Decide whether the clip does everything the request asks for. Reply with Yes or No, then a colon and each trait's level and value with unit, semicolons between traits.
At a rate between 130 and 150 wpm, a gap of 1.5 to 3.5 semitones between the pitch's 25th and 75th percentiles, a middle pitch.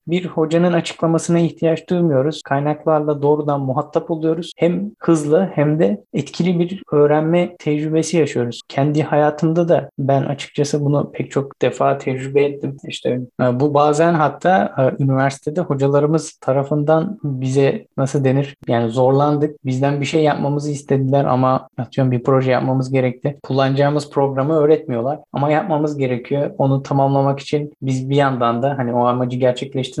Yes: fast, 140 wpm; average, 2.8 semitones; medium, 145 Hz